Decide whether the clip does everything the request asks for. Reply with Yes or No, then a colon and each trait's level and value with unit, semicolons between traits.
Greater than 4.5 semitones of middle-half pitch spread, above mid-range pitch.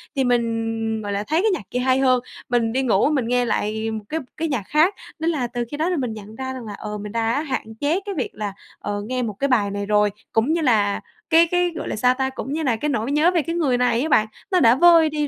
Yes: wide, 5.4 semitones; very high, 250 Hz